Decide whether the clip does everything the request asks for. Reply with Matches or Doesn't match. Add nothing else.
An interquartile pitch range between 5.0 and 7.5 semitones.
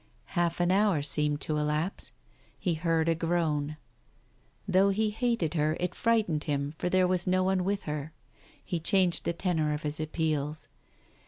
Doesn't match